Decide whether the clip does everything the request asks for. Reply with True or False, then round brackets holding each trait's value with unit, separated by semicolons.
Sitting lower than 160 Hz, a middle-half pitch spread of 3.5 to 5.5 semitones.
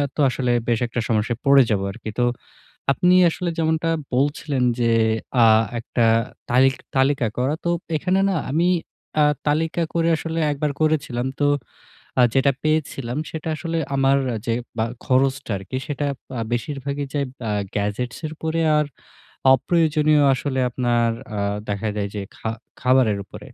True (135 Hz; 4.2 semitones)